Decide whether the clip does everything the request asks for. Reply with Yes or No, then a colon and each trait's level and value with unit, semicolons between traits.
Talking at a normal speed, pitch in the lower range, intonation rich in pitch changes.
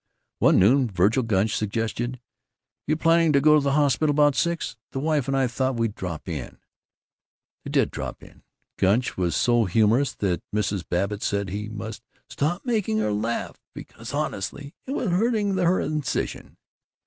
Yes: average, 165 wpm; low, 120 Hz; wide, 6.5 semitones